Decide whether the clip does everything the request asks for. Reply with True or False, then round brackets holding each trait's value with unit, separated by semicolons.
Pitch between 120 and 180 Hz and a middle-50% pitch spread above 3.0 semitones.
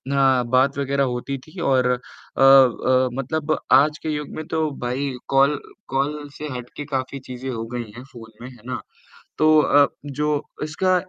False (135 Hz; 2.6 semitones)